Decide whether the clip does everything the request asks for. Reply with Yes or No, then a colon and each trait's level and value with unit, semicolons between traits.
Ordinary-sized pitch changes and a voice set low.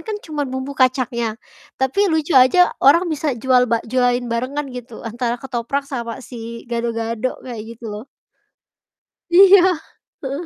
No: average, 3.3 semitones; very high, 255 Hz